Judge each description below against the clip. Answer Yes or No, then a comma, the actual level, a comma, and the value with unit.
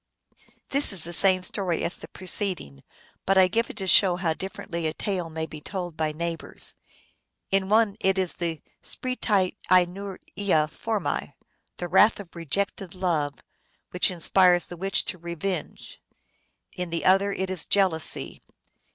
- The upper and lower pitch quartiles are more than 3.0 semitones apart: No, narrow, 2.5 semitones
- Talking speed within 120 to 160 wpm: Yes, average, 155 wpm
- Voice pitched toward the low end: No, medium, 185 Hz